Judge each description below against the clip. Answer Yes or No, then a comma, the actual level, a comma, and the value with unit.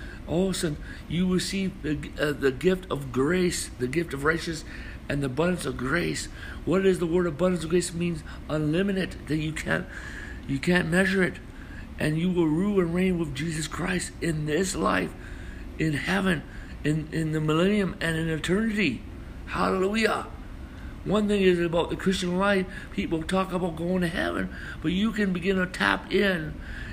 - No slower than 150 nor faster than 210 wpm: Yes, average, 180 wpm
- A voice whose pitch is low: No, medium, 170 Hz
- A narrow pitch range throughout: No, average, 3.3 semitones